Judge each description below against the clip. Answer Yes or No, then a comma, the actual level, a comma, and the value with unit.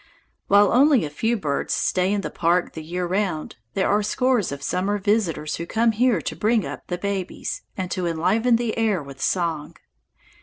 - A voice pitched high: Yes, high, 195 Hz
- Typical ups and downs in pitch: Yes, average, 4.6 semitones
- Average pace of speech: Yes, average, 190 wpm